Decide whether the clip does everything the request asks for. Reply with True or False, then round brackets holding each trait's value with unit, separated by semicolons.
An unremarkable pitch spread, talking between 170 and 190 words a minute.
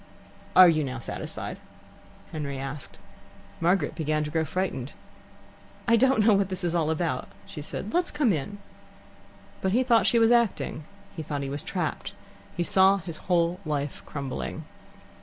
False (4.9 semitones; 160 wpm)